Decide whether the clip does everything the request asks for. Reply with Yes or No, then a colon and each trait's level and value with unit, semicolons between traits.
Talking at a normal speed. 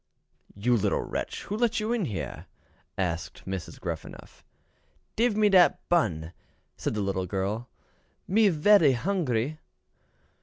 No: slow, 120 wpm